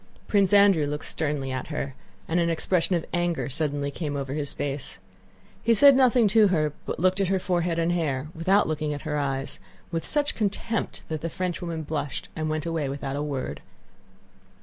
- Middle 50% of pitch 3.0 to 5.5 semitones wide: Yes, average, 4.2 semitones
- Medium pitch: Yes, medium, 160 Hz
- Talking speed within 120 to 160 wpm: No, average, 190 wpm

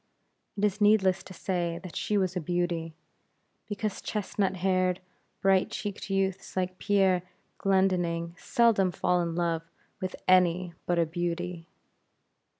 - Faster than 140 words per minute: No, slow, 135 wpm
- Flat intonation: Yes, narrow, 1.9 semitones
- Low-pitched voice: No, medium, 185 Hz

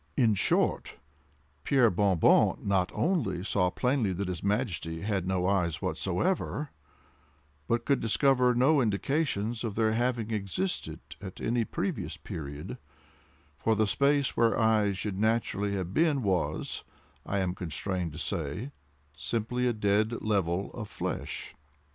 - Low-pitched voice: Yes, low, 105 Hz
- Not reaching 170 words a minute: Yes, slow, 135 wpm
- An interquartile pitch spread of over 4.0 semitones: Yes, average, 4.4 semitones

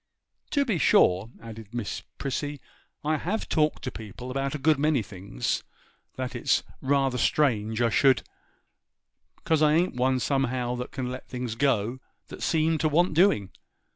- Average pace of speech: Yes, average, 160 wpm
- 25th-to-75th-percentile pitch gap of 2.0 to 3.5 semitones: No, average, 4.3 semitones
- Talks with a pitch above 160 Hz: No, low, 130 Hz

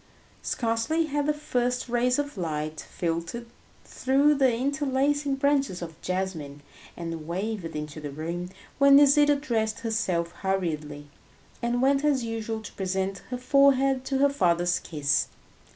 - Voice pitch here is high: Yes, high, 230 Hz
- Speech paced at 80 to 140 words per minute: Yes, slow, 135 wpm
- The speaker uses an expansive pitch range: Yes, wide, 8.3 semitones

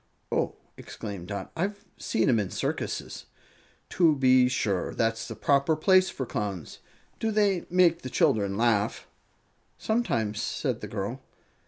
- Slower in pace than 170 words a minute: Yes, average, 140 wpm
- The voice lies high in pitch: No, low, 130 Hz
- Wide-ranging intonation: Yes, wide, 9.0 semitones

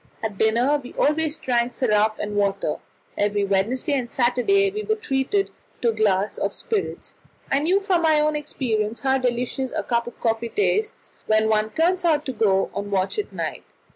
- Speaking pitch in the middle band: No, high, 245 Hz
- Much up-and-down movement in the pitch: Yes, wide, 6.0 semitones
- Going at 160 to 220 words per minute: Yes, average, 185 wpm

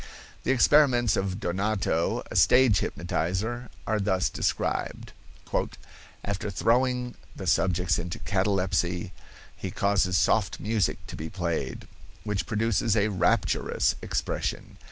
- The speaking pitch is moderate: No, low, 100 Hz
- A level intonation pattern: No, average, 3.7 semitones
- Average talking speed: No, slow, 115 wpm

